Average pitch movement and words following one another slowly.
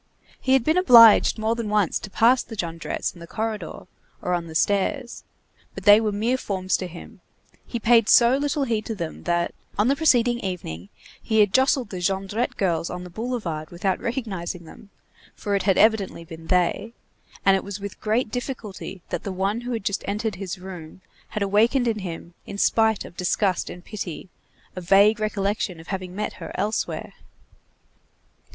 No: average, 3.9 semitones; average, 185 wpm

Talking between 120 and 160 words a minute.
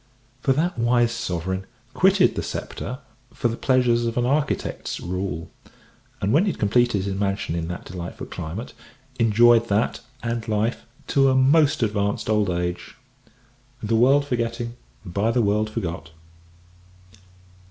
Yes: average, 140 wpm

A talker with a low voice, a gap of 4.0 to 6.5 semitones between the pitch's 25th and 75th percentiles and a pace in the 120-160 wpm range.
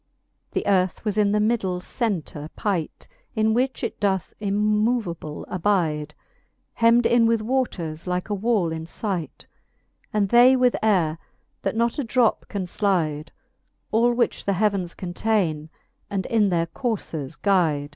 No: high, 200 Hz; average, 4.7 semitones; average, 145 wpm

